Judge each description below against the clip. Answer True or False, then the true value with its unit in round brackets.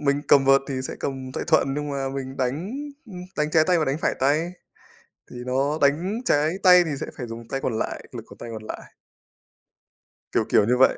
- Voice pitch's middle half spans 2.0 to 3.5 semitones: True (3.1 semitones)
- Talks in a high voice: False (140 Hz)